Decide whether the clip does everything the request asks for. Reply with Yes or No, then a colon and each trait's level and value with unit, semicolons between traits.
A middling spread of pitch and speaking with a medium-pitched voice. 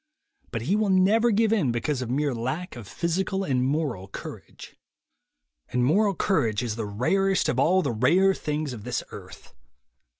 No: wide, 7.8 semitones; medium, 150 Hz